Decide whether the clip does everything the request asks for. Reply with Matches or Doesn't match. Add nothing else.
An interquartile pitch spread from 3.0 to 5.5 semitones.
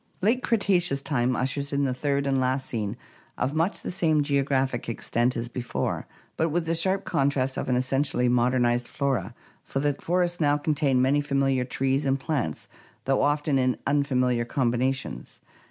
Doesn't match